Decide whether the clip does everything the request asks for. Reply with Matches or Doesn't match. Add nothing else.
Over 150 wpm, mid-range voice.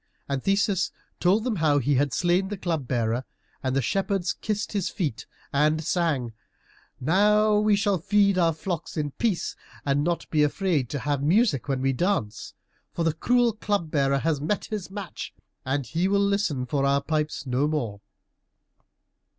Matches